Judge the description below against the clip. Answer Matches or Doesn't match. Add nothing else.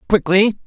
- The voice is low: Doesn't match